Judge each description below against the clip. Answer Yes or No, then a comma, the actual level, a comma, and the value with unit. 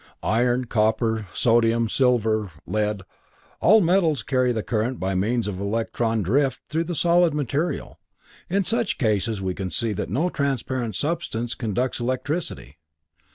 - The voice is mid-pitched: No, low, 120 Hz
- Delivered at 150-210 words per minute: No, average, 140 wpm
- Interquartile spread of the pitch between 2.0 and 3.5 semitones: No, average, 5.0 semitones